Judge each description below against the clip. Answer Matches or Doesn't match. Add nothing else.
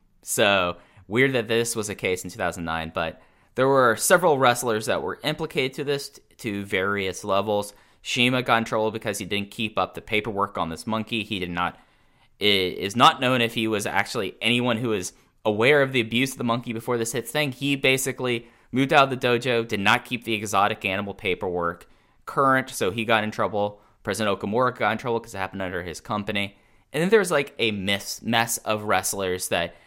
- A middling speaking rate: Doesn't match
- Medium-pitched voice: Doesn't match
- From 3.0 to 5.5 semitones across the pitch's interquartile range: Matches